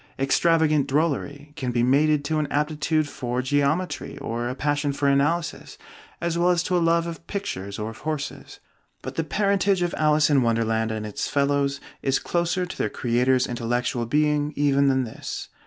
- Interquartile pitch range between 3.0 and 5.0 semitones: Yes, average, 3.9 semitones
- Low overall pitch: No, medium, 145 Hz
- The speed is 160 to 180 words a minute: Yes, average, 175 wpm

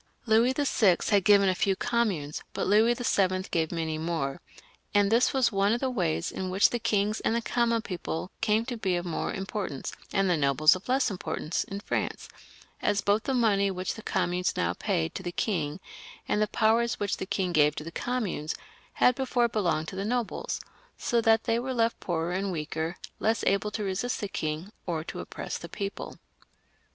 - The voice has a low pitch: No, high, 200 Hz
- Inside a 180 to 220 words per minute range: Yes, average, 200 wpm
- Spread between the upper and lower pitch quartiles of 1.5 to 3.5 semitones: No, average, 4.6 semitones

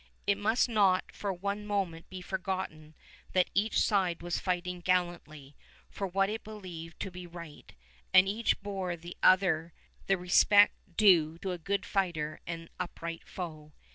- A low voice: No, medium, 180 Hz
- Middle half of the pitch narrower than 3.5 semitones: Yes, average, 2.8 semitones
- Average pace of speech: Yes, average, 150 wpm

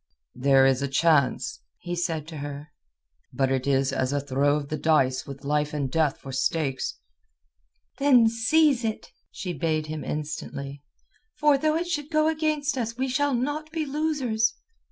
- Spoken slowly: No, average, 170 wpm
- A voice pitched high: No, medium, 160 Hz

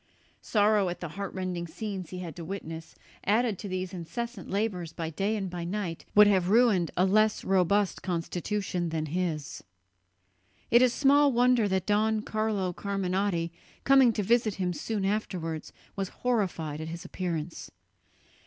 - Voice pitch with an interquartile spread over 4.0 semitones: No, average, 3.6 semitones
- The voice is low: No, high, 190 Hz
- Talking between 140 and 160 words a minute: Yes, average, 155 wpm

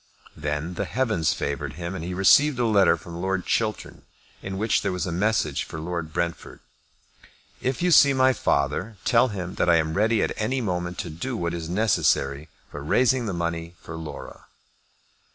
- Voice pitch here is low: Yes, very low, 90 Hz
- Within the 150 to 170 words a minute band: No, average, 185 wpm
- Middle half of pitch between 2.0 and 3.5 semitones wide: No, average, 5.1 semitones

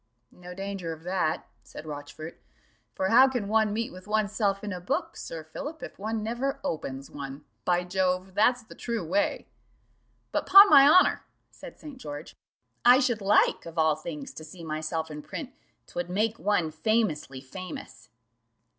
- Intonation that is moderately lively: No, wide, 5.8 semitones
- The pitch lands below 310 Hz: Yes, medium, 185 Hz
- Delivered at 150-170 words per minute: Yes, average, 165 wpm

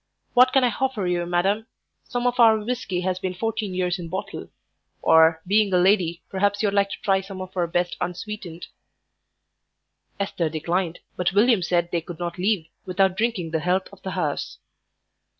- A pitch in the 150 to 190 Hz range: Yes, medium, 185 Hz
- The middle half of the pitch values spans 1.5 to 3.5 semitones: Yes, average, 3.0 semitones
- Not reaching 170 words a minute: No, average, 180 wpm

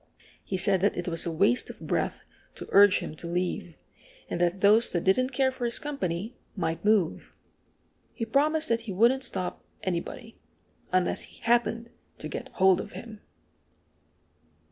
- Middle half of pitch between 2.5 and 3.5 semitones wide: No, average, 4.8 semitones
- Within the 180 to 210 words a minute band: No, average, 165 wpm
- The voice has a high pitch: Yes, high, 205 Hz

